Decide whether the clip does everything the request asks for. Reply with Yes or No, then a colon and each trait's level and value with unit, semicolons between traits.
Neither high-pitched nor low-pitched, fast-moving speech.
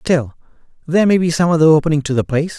Yes: medium, 160 Hz; fast, 230 wpm